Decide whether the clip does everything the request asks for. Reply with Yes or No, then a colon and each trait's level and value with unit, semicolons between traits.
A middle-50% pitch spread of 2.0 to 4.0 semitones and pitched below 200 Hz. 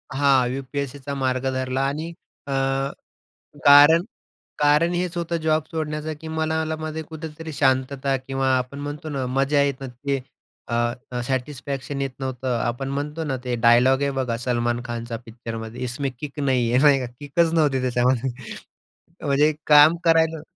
Yes: average, 3.0 semitones; medium, 140 Hz